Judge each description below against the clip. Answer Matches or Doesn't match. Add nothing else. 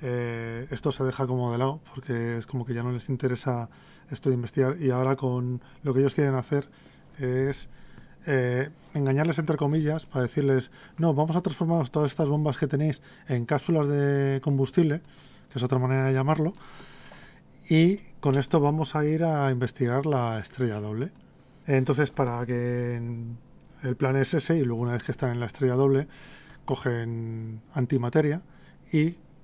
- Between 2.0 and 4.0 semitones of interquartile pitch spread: Matches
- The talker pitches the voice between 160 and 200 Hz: Doesn't match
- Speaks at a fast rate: Doesn't match